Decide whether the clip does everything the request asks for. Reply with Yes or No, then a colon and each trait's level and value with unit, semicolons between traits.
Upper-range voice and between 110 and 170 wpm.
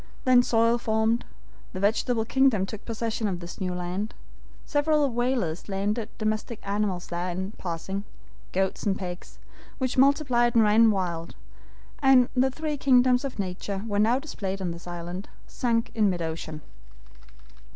Yes: high, 215 Hz; average, 150 wpm